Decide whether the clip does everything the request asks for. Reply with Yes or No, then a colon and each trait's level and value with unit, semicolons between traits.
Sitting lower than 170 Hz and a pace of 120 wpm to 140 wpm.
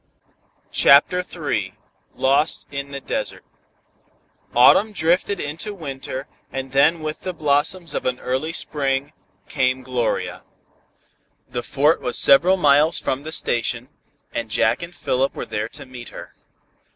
Yes: medium, 140 Hz; slow, 135 wpm